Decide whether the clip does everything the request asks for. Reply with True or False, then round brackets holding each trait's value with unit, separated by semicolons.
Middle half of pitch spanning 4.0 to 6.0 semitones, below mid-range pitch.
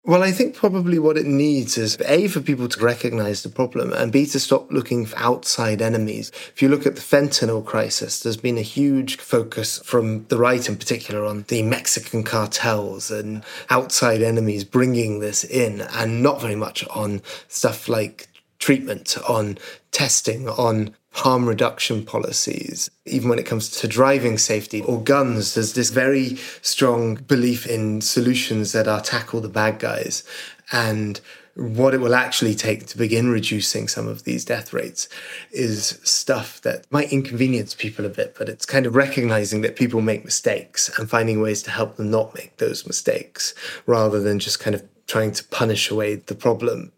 False (3.2 semitones; 115 Hz)